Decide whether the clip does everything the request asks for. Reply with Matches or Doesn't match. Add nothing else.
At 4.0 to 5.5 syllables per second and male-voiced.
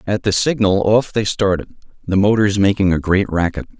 Matches